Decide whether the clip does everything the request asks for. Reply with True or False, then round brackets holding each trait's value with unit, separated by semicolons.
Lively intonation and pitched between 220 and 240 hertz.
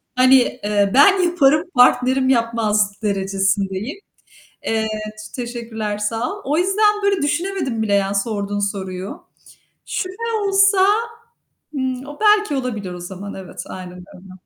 True (6.5 semitones; 230 Hz)